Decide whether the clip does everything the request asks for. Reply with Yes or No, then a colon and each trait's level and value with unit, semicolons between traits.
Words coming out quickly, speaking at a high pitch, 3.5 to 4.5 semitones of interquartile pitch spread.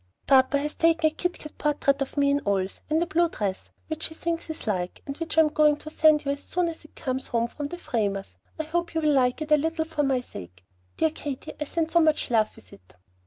Yes: fast, 260 wpm; very high, 300 Hz; average, 3.9 semitones